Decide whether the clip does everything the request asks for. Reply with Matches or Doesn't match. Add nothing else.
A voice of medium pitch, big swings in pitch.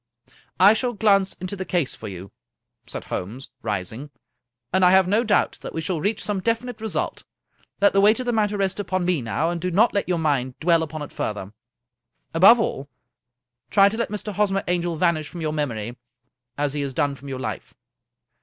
Matches